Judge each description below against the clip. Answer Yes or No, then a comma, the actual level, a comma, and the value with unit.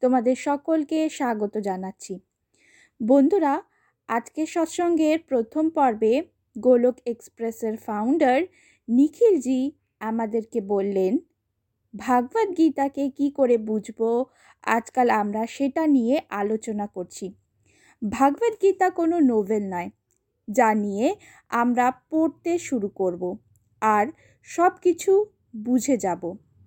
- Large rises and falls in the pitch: Yes, wide, 6.4 semitones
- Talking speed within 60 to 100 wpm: Yes, average, 95 wpm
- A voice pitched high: Yes, very high, 250 Hz